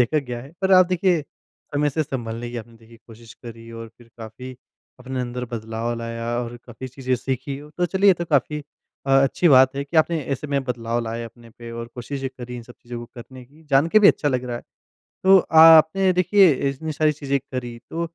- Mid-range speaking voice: No, low, 130 Hz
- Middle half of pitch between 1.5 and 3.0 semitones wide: No, average, 4.5 semitones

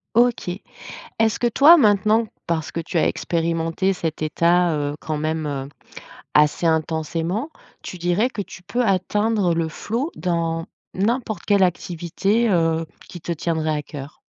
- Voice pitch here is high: No, medium, 175 Hz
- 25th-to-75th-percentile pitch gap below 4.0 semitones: No, average, 4.5 semitones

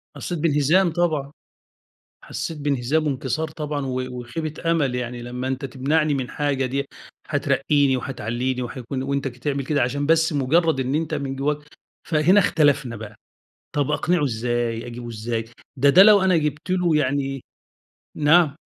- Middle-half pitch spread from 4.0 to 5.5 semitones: No, average, 3.4 semitones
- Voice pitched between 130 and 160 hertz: Yes, medium, 140 Hz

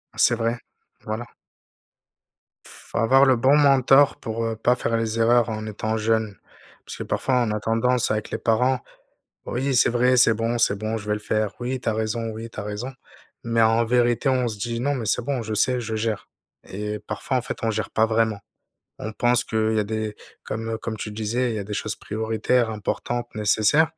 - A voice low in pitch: Yes, low, 115 Hz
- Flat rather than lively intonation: Yes, narrow, 2.0 semitones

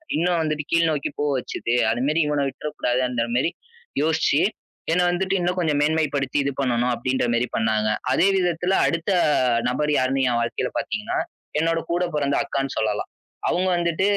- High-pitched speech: No, medium, 145 Hz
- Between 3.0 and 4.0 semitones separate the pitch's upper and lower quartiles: No, average, 4.8 semitones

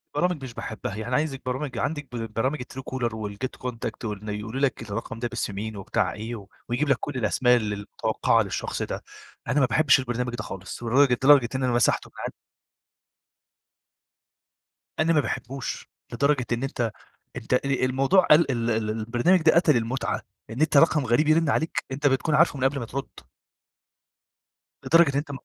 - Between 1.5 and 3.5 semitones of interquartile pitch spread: No, average, 3.9 semitones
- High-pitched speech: No, low, 125 Hz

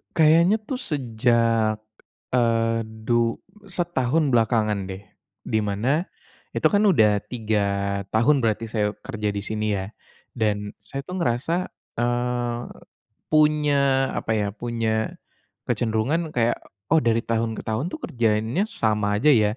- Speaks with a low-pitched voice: Yes, low, 115 Hz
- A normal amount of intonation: Yes, average, 4.3 semitones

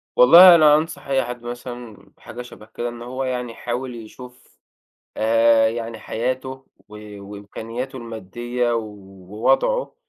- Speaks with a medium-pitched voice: No, low, 120 Hz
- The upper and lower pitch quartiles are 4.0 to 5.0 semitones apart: No, narrow, 2.4 semitones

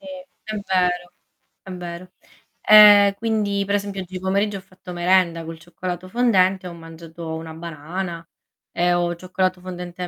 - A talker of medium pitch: Yes, medium, 180 Hz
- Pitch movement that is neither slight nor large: No, narrow, 2.1 semitones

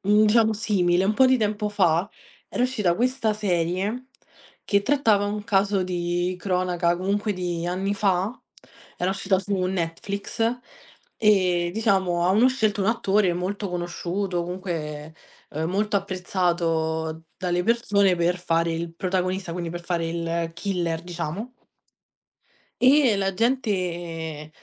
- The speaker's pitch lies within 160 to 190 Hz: Yes, medium, 185 Hz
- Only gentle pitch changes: No, average, 3.1 semitones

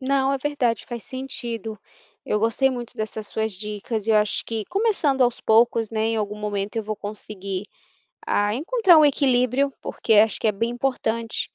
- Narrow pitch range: No, average, 3.7 semitones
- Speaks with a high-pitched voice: Yes, high, 230 Hz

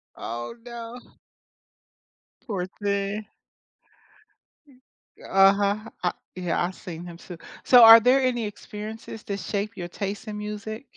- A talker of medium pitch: No, high, 210 Hz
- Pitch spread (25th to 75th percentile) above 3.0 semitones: No, average, 2.7 semitones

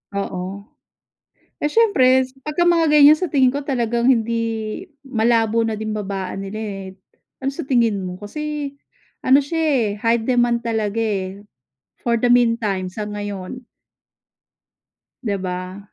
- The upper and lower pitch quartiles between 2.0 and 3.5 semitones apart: No, average, 4.3 semitones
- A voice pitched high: Yes, high, 230 Hz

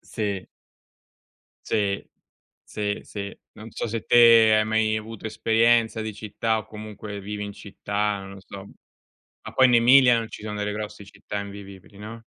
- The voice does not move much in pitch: Yes, narrow, 1.6 semitones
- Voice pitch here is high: No, low, 105 Hz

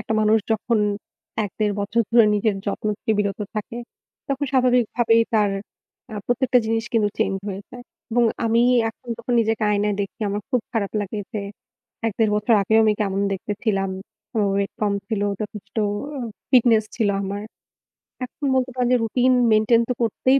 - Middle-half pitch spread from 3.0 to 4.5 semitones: No, narrow, 2.6 semitones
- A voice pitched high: Yes, high, 220 Hz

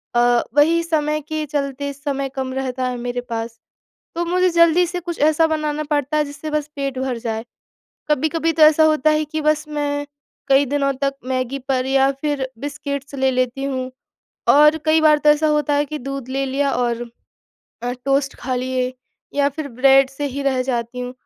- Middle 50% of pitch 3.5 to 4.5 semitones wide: No, average, 2.8 semitones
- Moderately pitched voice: No, very high, 280 Hz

